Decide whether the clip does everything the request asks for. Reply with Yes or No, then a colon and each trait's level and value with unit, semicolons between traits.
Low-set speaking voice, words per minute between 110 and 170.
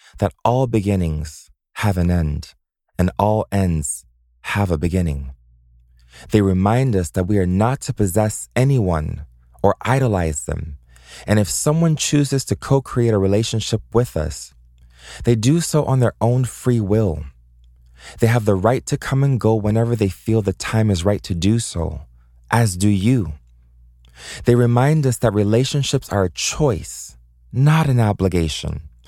Yes: low, 100 Hz; average, 155 wpm